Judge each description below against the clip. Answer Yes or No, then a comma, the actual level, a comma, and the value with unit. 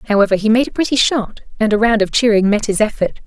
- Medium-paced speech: No, fast, 260 wpm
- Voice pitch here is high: Yes, high, 220 Hz